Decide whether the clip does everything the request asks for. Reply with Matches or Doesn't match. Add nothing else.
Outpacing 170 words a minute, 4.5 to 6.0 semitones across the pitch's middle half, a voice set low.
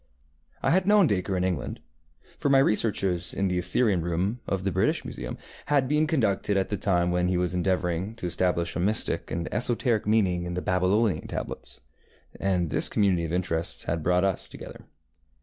Doesn't match